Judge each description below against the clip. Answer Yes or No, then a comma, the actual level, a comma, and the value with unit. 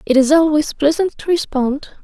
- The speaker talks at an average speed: Yes, average, 175 wpm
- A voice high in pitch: Yes, very high, 300 Hz